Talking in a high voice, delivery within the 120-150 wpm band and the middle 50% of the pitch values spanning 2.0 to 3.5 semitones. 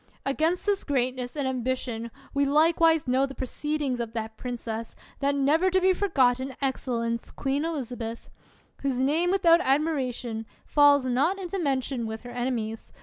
No: very high, 270 Hz; average, 145 wpm; average, 4.0 semitones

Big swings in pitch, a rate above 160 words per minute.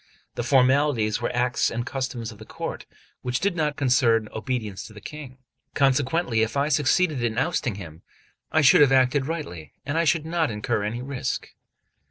No: average, 4.4 semitones; average, 175 wpm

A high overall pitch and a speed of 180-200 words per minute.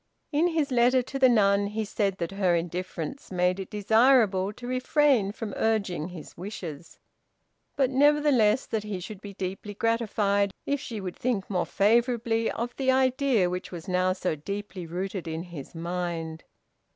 No: high, 205 Hz; average, 165 wpm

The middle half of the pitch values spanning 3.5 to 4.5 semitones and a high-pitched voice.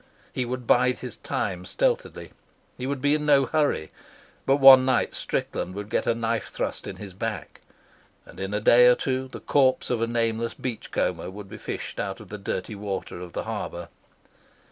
No: average, 4.2 semitones; low, 120 Hz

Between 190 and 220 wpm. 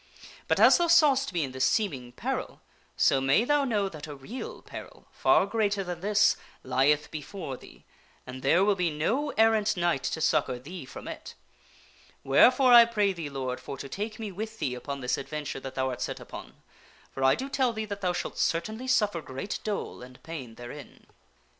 Yes: fast, 205 wpm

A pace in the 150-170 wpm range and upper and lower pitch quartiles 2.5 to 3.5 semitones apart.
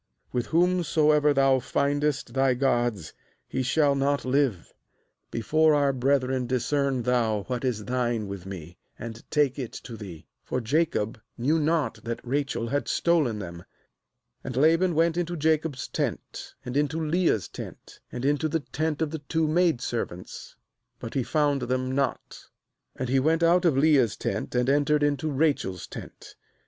No: average, 160 wpm; average, 4.0 semitones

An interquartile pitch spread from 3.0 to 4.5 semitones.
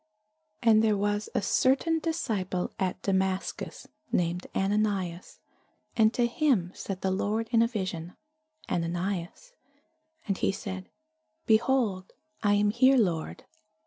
Yes: average, 3.4 semitones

